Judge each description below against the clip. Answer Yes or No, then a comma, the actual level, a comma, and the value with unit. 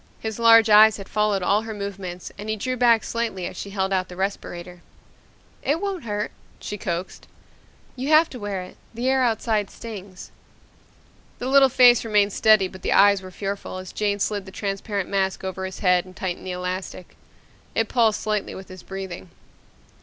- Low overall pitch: No, high, 200 Hz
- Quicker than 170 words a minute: Yes, average, 185 wpm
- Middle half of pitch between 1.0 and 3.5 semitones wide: Yes, average, 3.0 semitones